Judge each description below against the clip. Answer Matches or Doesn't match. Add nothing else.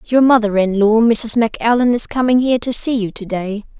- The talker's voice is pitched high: Matches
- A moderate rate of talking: Doesn't match